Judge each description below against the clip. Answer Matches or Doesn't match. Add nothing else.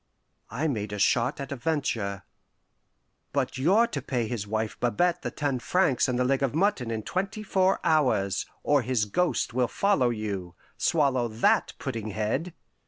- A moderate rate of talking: Matches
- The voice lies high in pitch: Doesn't match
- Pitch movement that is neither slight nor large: Doesn't match